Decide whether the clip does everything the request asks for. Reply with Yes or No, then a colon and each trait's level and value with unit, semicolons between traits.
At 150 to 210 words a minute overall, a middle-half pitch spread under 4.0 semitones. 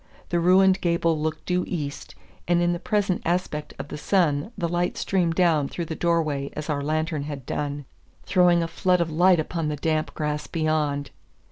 Yes: average, 195 wpm; average, 2.7 semitones